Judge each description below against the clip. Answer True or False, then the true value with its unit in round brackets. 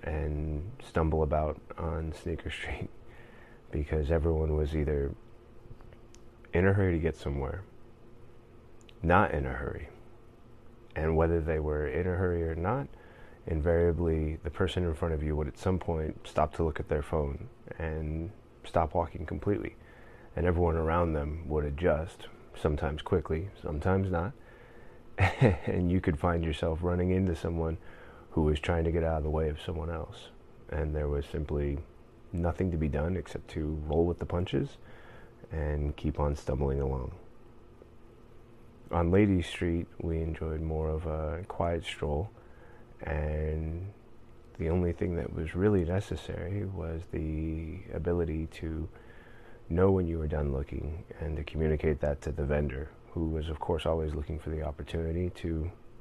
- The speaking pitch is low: True (85 Hz)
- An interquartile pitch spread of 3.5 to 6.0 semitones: True (4.0 semitones)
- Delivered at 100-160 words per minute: True (155 wpm)